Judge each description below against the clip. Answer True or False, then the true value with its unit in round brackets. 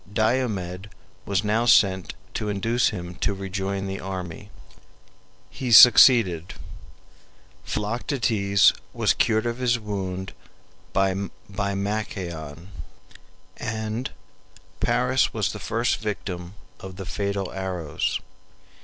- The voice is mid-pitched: False (100 Hz)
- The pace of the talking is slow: True (100 wpm)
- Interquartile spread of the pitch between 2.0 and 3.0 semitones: True (2.7 semitones)